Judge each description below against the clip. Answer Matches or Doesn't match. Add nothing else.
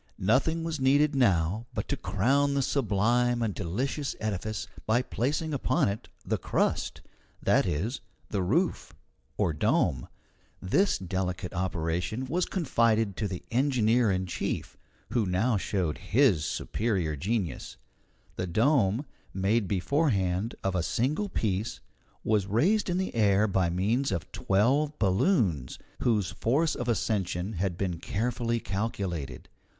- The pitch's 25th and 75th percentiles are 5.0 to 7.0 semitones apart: Matches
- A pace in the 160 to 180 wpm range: Doesn't match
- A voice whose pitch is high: Doesn't match